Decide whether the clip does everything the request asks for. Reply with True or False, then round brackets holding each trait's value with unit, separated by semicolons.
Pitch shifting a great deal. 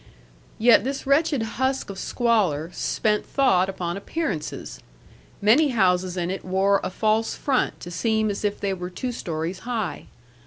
False (4.9 semitones)